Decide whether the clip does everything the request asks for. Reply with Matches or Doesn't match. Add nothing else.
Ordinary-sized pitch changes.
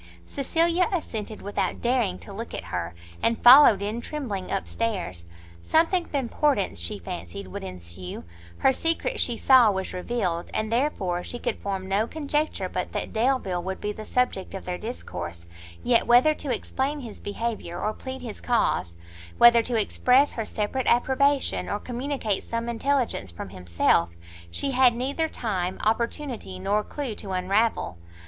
Doesn't match